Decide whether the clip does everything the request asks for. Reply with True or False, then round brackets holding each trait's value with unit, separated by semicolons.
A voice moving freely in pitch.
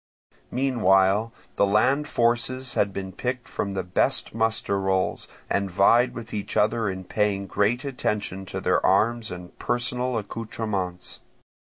False (3.7 semitones)